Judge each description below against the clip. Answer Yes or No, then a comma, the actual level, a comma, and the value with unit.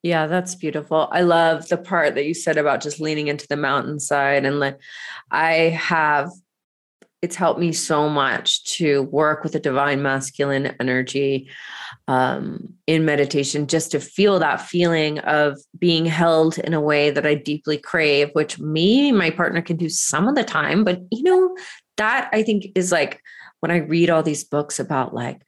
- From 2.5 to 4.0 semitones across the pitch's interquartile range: Yes, average, 3.0 semitones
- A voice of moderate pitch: Yes, medium, 155 Hz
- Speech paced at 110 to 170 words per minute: No, average, 180 wpm